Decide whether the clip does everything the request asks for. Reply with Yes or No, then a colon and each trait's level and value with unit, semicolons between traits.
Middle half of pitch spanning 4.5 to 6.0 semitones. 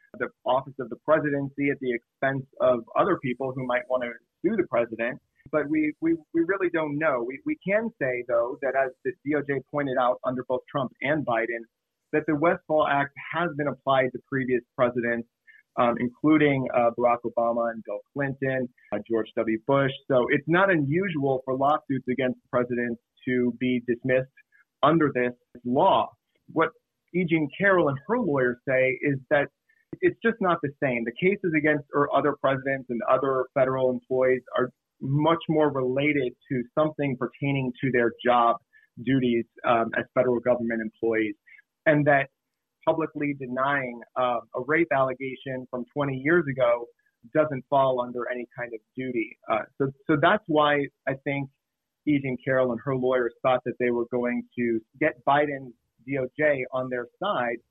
No: average, 3.3 semitones